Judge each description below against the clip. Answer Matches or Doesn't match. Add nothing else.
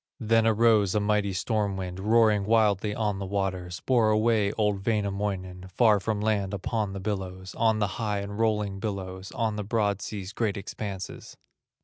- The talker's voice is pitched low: Matches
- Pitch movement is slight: Matches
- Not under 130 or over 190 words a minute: Matches